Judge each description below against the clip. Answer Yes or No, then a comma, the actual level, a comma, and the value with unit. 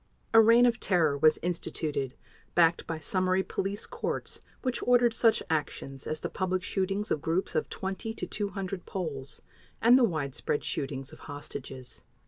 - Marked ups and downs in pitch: Yes, wide, 5.8 semitones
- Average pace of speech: Yes, average, 155 wpm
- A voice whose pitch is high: No, medium, 180 Hz